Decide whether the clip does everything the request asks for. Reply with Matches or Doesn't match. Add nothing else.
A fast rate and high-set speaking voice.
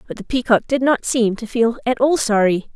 Matches